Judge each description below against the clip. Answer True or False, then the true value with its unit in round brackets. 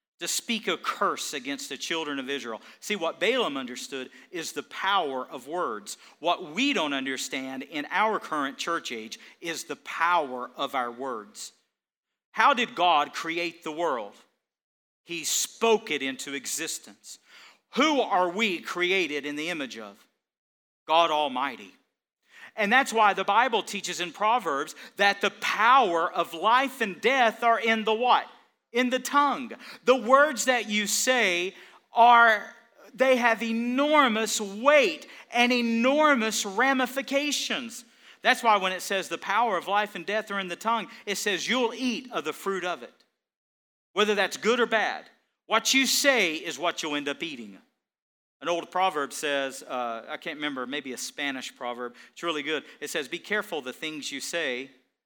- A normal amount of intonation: False (7.5 semitones)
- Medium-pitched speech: False (195 Hz)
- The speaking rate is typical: True (165 wpm)